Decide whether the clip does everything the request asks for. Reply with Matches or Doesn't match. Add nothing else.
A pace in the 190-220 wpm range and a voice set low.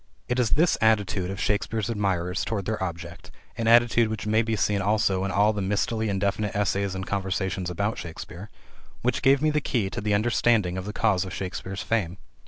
Matches